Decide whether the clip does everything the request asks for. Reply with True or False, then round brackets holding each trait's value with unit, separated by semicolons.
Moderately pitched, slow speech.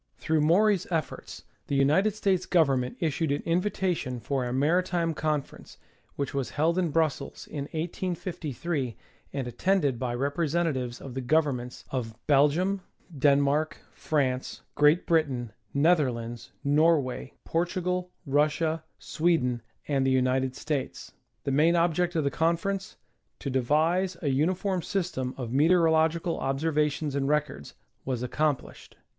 True (150 Hz; 130 wpm)